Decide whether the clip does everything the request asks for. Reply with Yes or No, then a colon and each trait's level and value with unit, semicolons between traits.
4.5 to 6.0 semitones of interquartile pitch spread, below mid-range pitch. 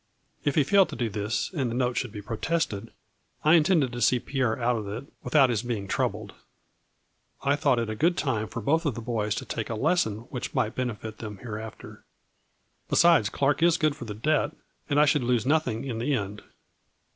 Yes: average, 4.9 semitones; low, 125 Hz